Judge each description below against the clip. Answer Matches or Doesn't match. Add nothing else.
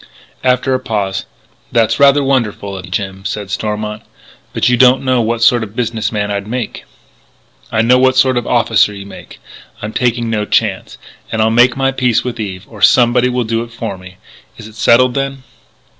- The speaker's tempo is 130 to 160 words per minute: Doesn't match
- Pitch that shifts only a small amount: Doesn't match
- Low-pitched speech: Matches